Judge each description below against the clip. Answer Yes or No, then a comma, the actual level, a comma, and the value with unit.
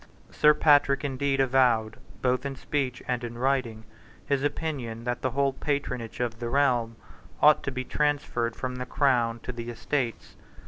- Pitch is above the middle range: No, low, 130 Hz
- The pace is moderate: Yes, average, 165 wpm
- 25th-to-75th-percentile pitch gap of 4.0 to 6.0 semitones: No, average, 2.9 semitones